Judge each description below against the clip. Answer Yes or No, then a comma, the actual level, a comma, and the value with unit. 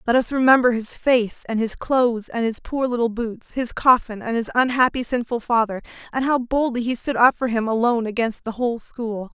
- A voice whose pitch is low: No, high, 235 Hz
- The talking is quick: Yes, fast, 210 wpm